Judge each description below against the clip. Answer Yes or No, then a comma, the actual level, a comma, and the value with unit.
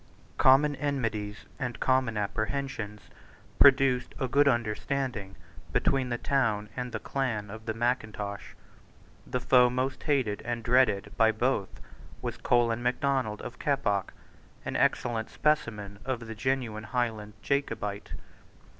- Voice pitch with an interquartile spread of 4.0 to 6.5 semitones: No, average, 3.6 semitones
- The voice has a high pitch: No, low, 120 Hz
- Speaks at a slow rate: Yes, slow, 120 wpm